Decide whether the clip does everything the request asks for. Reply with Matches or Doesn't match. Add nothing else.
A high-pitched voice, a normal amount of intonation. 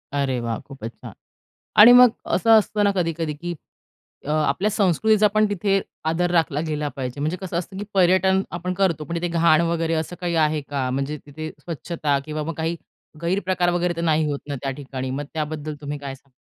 Doesn't match